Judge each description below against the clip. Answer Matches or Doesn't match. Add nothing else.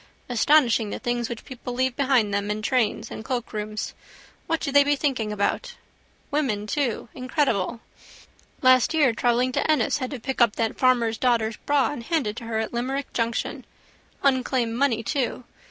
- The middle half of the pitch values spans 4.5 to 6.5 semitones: Doesn't match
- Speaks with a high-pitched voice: Matches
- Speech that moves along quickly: Doesn't match